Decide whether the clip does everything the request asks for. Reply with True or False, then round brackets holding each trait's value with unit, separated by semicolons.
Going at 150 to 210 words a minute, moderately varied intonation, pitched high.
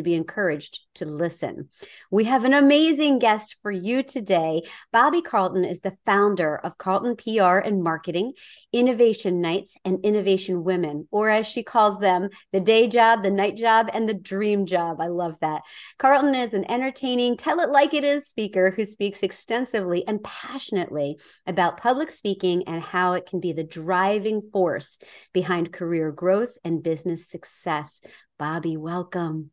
True (165 wpm; 4.7 semitones; 195 Hz)